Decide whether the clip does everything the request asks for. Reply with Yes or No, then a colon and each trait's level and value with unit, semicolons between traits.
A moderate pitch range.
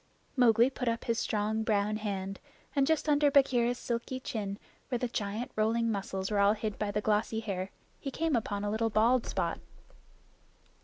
Yes: average, 3.0 semitones